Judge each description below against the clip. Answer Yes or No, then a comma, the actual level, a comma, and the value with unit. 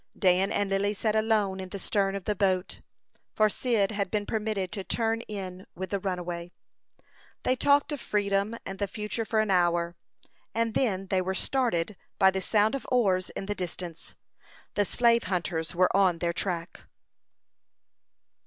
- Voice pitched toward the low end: No, high, 195 Hz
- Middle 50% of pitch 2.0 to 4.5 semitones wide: Yes, average, 2.7 semitones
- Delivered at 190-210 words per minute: No, average, 170 wpm